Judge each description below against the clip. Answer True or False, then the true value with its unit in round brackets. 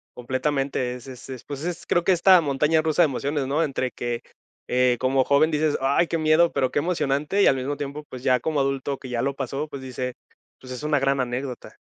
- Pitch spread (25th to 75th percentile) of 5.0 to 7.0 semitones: False (2.8 semitones)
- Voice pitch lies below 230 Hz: True (140 Hz)